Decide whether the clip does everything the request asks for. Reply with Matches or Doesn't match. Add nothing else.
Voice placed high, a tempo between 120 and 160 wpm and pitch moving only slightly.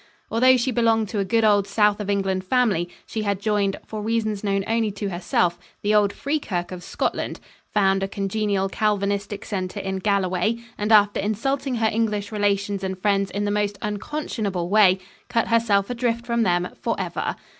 Doesn't match